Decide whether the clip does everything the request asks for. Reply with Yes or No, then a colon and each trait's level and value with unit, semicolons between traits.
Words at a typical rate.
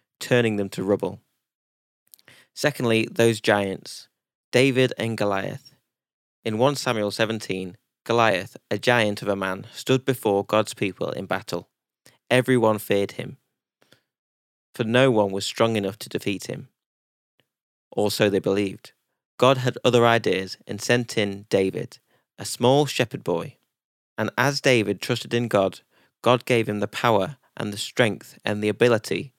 Yes: average, 145 wpm